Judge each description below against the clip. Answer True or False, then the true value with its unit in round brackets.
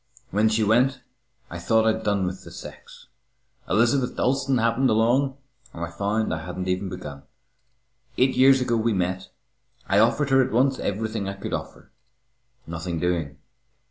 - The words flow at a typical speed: True (160 wpm)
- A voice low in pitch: True (110 Hz)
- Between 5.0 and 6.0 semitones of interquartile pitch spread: True (5.4 semitones)